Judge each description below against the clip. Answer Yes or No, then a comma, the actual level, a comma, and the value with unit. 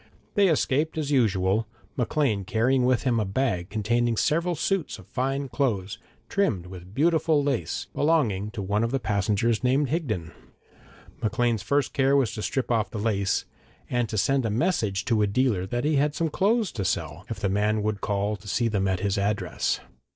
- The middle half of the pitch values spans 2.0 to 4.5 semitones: No, average, 5.3 semitones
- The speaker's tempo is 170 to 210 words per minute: Yes, average, 190 wpm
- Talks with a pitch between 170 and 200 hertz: No, low, 115 Hz